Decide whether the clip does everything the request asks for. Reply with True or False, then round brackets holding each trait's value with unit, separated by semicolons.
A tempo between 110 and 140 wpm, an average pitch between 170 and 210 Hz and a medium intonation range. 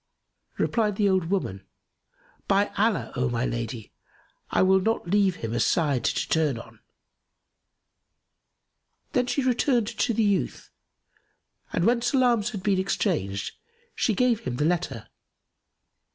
False (135 wpm; 190 Hz; 8.7 semitones)